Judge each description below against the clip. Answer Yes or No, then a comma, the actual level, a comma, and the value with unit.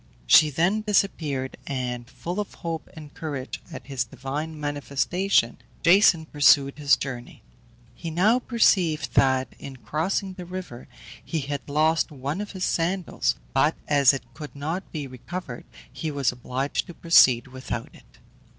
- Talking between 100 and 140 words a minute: No, average, 150 wpm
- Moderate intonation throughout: Yes, average, 4.6 semitones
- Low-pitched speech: No, medium, 150 Hz